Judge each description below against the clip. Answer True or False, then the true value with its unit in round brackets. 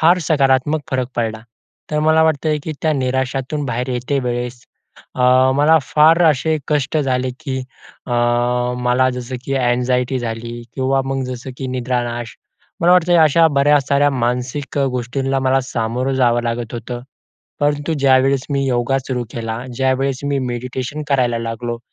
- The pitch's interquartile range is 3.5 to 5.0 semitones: False (2.5 semitones)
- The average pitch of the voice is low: True (130 Hz)